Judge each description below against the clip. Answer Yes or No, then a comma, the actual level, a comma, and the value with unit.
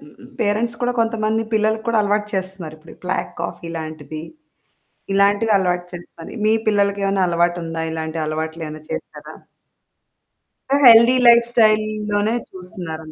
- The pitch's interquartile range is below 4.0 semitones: No, average, 4.9 semitones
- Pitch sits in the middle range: No, high, 195 Hz